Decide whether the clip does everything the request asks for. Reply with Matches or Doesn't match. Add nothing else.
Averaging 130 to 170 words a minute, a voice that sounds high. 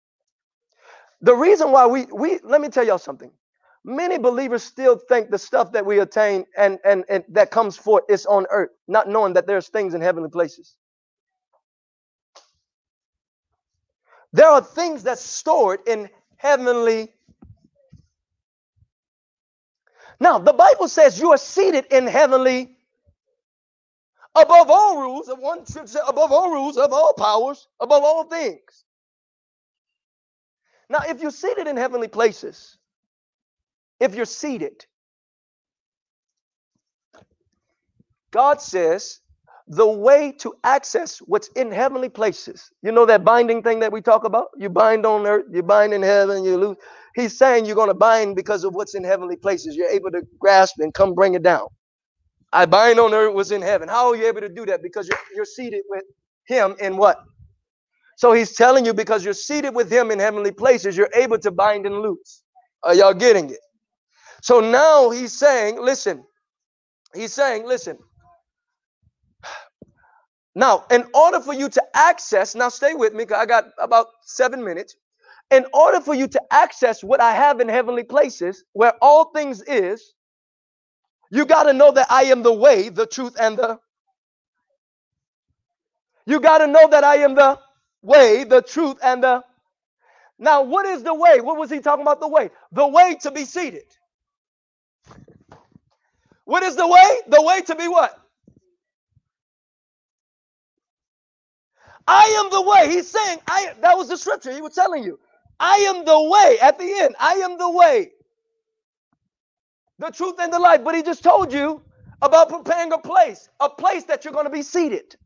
Matches